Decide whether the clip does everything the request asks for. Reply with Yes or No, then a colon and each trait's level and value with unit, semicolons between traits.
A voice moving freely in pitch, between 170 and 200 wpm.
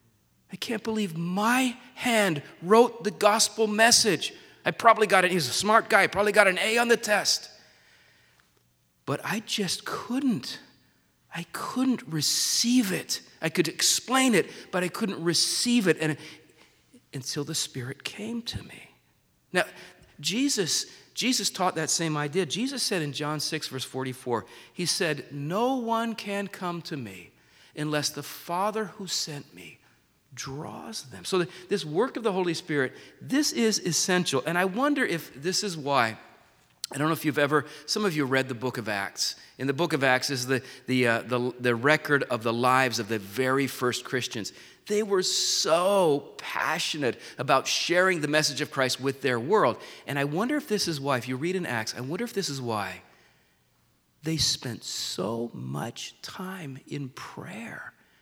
Yes: wide, 7.6 semitones; average, 175 wpm